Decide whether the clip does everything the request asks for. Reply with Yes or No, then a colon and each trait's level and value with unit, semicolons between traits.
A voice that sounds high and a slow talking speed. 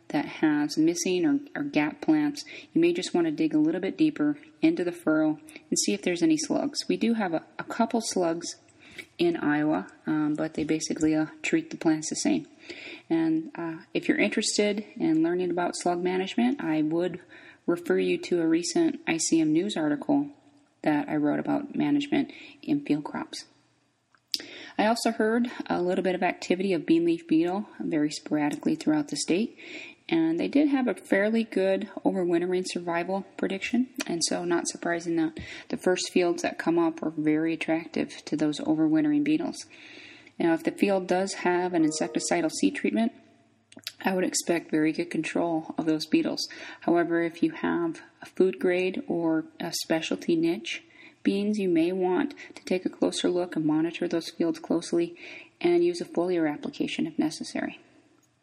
No: very high, 295 Hz; average, 175 wpm